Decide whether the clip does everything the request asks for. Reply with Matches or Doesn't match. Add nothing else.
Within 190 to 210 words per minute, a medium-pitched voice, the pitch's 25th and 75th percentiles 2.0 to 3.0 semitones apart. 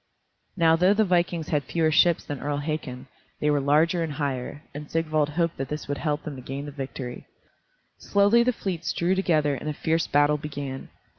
Matches